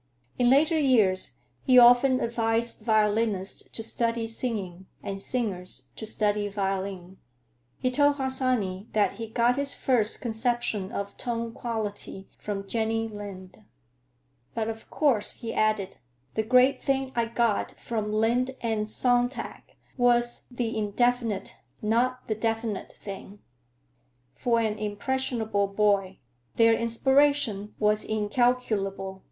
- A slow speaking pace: Yes, slow, 120 wpm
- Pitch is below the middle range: No, high, 225 Hz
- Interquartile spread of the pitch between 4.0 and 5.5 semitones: No, average, 3.0 semitones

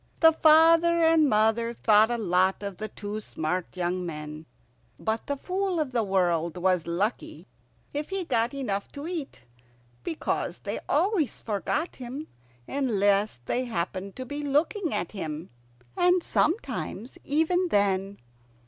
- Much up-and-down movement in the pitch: Yes, wide, 8.4 semitones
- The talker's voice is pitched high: Yes, high, 230 Hz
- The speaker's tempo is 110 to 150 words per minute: Yes, average, 140 wpm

